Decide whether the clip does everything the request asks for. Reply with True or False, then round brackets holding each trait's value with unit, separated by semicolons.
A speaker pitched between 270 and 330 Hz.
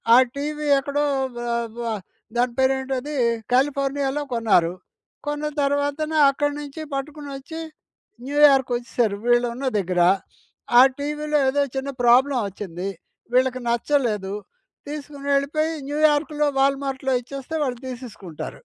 True (275 Hz)